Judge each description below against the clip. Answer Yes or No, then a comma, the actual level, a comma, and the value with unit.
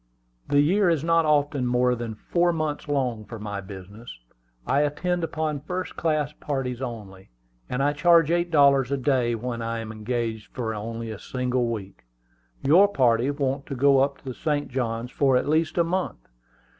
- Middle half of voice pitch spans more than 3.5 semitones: Yes, average, 4.6 semitones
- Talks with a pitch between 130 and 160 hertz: Yes, low, 135 Hz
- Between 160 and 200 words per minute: Yes, average, 180 wpm